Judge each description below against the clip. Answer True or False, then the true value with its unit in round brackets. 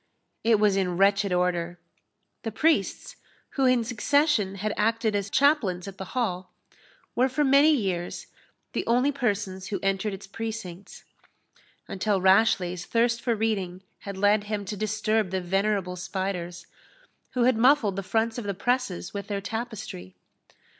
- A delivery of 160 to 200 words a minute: False (150 wpm)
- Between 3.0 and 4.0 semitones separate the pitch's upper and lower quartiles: True (3.4 semitones)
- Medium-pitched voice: False (205 Hz)